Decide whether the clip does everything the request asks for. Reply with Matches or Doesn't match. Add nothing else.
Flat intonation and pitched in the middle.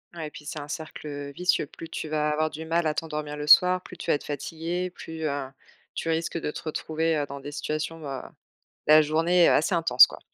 Matches